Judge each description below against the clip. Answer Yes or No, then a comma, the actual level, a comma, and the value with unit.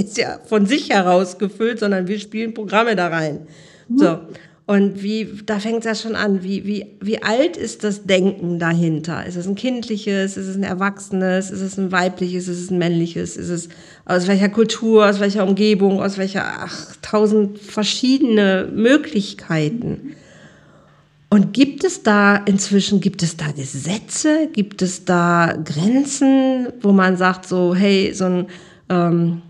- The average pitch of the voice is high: Yes, high, 195 Hz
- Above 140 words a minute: Yes, average, 160 wpm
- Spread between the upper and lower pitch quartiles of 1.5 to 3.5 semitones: Yes, average, 2.9 semitones